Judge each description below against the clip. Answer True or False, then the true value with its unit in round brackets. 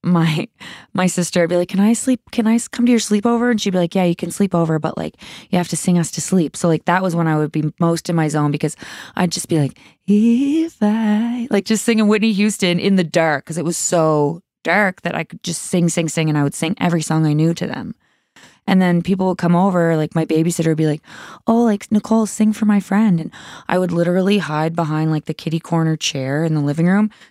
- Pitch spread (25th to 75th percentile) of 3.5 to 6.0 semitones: True (4.0 semitones)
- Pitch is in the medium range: True (175 Hz)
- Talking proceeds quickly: True (255 wpm)